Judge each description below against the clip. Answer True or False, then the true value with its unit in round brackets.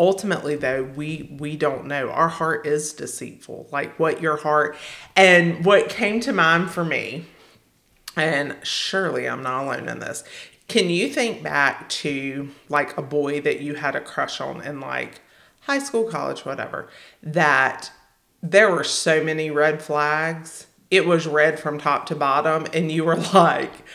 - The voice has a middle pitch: True (155 Hz)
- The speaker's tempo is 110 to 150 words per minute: False (165 wpm)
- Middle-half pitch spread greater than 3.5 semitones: False (2.8 semitones)